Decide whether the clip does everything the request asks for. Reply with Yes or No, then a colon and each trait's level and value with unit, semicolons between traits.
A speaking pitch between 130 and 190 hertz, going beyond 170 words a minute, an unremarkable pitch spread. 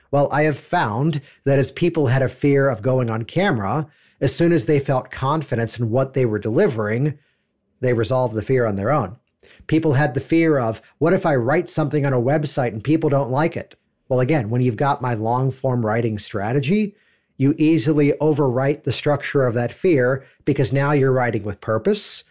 Yes: medium, 140 Hz; average, 200 wpm; average, 3.6 semitones